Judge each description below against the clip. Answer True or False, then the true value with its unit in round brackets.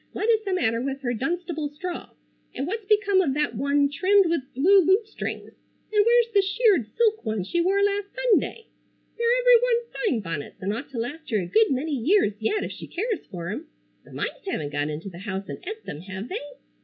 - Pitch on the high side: True (330 Hz)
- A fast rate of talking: True (215 wpm)